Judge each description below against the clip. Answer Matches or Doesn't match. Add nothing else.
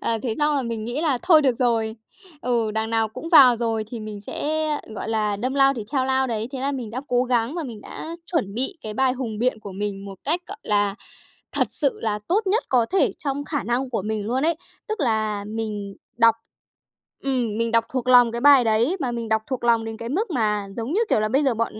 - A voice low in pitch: Doesn't match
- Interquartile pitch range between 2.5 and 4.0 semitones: Matches